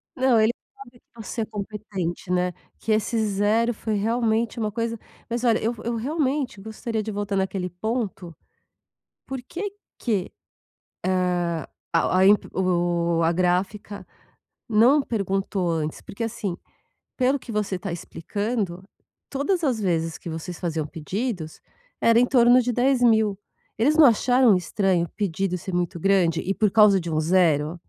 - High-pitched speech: Yes, high, 210 Hz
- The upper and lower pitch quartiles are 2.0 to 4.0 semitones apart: No, average, 4.6 semitones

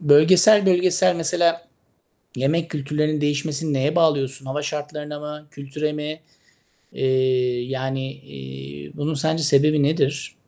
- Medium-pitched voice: Yes, medium, 150 Hz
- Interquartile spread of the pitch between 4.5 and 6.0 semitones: No, average, 2.8 semitones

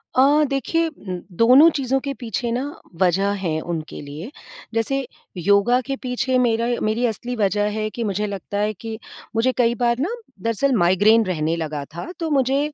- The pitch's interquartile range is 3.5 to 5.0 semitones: Yes, average, 4.7 semitones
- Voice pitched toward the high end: Yes, high, 230 Hz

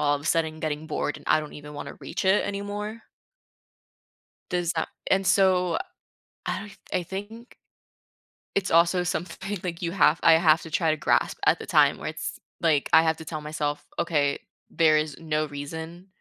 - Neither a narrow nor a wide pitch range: Yes, average, 3.4 semitones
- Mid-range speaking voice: Yes, medium, 165 Hz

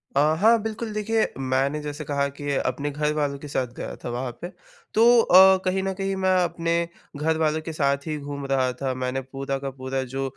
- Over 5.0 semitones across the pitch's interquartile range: Yes, wide, 5.4 semitones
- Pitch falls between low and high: Yes, medium, 150 Hz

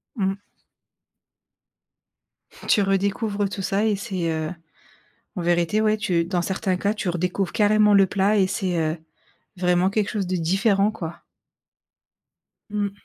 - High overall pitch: Yes, high, 195 Hz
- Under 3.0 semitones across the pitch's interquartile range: Yes, narrow, 2.6 semitones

